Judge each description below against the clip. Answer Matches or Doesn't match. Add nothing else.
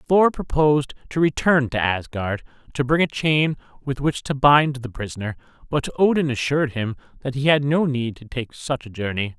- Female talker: Doesn't match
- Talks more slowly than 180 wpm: Doesn't match